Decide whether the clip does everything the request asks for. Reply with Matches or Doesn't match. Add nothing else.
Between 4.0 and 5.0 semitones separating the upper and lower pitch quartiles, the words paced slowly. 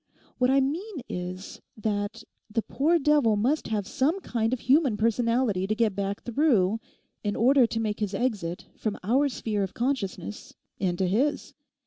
Doesn't match